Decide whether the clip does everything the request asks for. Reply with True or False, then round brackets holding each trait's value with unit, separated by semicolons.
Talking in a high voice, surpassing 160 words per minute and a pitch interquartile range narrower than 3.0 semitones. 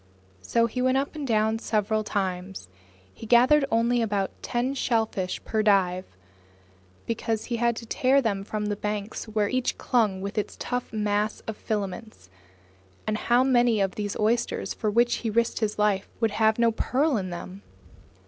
True (220 Hz; 170 wpm; 2.6 semitones)